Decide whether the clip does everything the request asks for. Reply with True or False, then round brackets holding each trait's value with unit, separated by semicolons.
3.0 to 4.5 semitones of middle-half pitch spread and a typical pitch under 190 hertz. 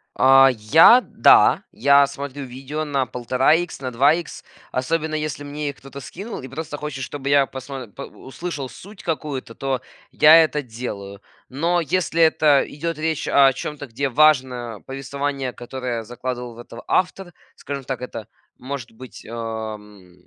True (3.3 semitones; 135 Hz)